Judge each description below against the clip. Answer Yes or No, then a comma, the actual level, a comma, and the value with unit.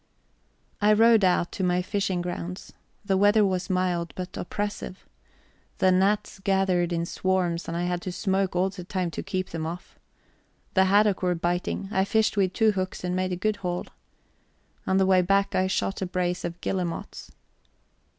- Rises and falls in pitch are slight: Yes, narrow, 1.6 semitones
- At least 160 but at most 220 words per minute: Yes, average, 180 wpm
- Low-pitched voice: No, medium, 185 Hz